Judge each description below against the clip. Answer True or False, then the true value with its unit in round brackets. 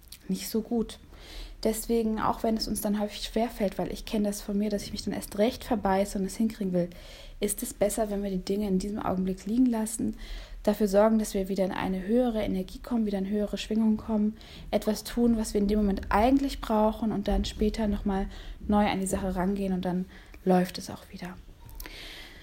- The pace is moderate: False (210 wpm)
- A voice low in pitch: False (210 Hz)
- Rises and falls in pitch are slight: True (2.2 semitones)